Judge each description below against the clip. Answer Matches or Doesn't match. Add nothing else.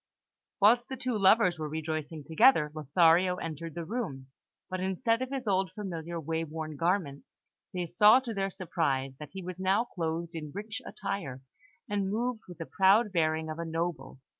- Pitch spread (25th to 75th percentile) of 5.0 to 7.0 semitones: Doesn't match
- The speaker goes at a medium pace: Matches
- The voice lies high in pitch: Doesn't match